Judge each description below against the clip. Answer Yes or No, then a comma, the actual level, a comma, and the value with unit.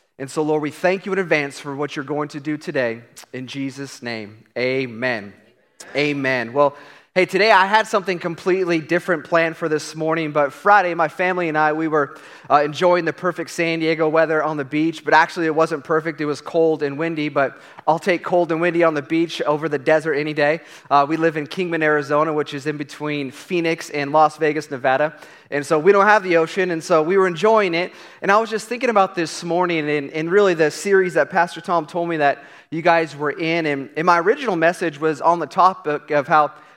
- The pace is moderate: No, fast, 220 wpm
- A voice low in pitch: No, medium, 160 Hz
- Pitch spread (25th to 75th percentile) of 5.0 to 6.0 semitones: No, narrow, 2.6 semitones